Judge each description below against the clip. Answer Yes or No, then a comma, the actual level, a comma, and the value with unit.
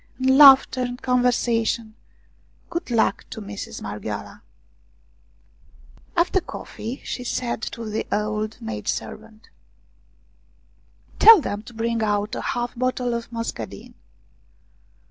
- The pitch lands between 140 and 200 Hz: No, high, 235 Hz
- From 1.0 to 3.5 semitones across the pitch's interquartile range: Yes, average, 2.7 semitones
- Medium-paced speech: No, slow, 120 wpm